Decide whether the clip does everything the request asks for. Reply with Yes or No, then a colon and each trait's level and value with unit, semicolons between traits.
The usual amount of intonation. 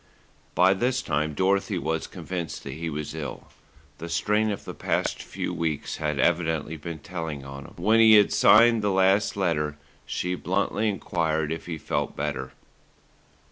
Yes: average, 4.3 semitones